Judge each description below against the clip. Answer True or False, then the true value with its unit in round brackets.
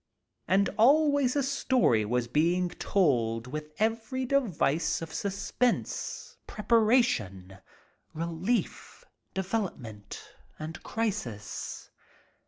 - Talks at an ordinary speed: False (80 wpm)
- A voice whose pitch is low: False (185 Hz)